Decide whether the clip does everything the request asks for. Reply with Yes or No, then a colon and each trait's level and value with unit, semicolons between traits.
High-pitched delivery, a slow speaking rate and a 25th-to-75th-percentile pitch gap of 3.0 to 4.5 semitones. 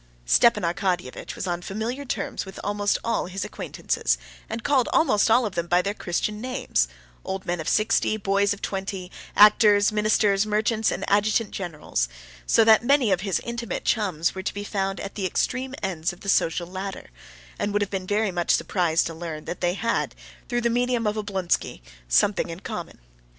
No: high, 200 Hz; average, 185 wpm; average, 3.3 semitones